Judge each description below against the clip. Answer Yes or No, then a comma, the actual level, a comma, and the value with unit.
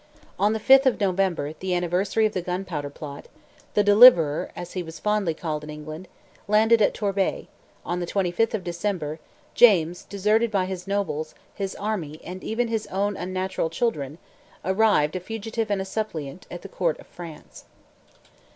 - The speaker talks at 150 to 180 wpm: Yes, average, 170 wpm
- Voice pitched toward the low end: No, high, 190 Hz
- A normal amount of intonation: Yes, average, 4.0 semitones